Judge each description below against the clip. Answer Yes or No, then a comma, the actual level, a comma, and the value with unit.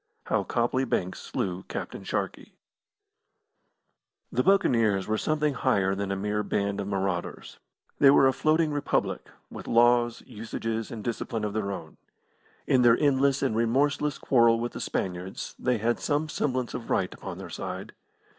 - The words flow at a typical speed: Yes, average, 160 wpm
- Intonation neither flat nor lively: Yes, average, 4.9 semitones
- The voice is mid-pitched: No, low, 115 Hz